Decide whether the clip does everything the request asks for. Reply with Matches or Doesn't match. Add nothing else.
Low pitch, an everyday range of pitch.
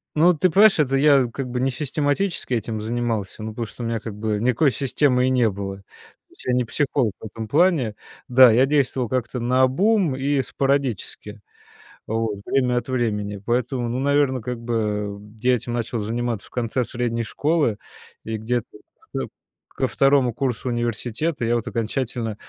Matches